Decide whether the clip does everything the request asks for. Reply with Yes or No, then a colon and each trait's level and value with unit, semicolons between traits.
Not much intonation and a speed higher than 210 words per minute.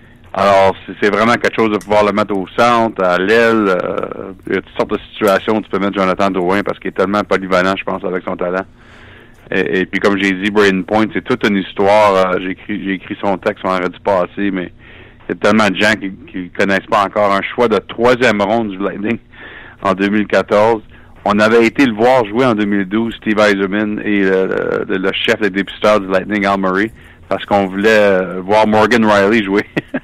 Yes: narrow, 2.2 semitones; fast, 220 wpm